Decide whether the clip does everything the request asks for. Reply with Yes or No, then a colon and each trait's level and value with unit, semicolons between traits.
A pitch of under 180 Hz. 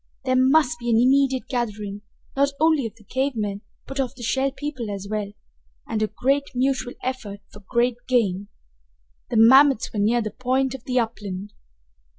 No: high, 245 Hz